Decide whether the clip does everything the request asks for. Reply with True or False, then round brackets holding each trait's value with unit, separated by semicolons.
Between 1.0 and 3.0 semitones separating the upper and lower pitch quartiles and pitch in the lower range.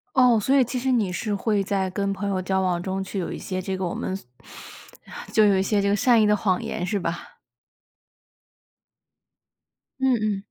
False (2.4 semitones; 200 Hz)